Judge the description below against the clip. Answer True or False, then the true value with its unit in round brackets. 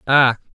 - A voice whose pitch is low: True (130 Hz)